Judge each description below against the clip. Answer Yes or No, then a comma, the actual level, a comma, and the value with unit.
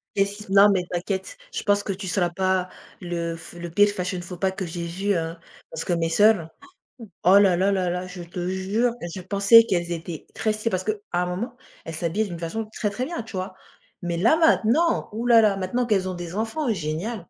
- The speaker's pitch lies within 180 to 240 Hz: Yes, high, 190 Hz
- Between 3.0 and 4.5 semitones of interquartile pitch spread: Yes, average, 3.5 semitones